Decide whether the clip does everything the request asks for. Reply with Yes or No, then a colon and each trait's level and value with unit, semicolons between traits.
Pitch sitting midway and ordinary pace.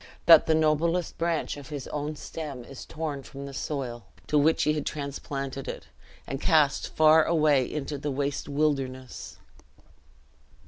Yes: medium, 145 Hz; average, 150 wpm